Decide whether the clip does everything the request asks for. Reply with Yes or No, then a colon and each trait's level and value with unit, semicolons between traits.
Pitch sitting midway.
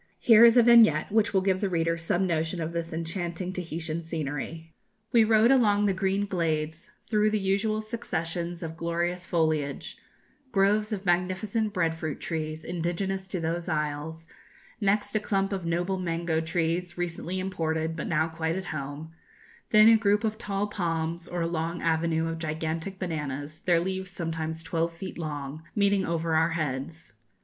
Yes: medium, 170 Hz